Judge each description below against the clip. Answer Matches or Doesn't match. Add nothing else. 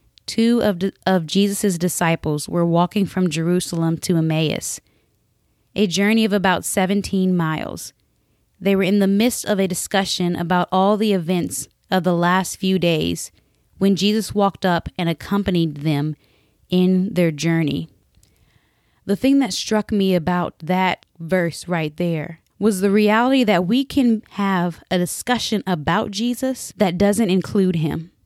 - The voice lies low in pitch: Doesn't match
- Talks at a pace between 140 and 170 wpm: Matches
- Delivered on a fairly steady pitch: Doesn't match